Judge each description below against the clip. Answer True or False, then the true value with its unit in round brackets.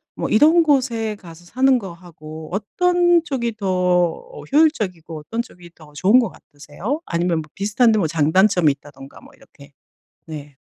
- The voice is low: False (185 Hz)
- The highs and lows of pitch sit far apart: True (7.6 semitones)